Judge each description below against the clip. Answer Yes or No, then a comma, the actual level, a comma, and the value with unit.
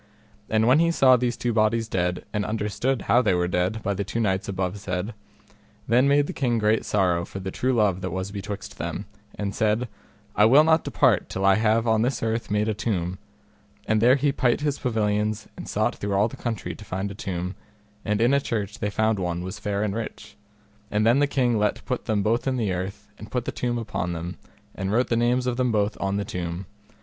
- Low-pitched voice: Yes, low, 105 Hz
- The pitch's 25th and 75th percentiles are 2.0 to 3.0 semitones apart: No, average, 3.5 semitones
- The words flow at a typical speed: No, fast, 230 wpm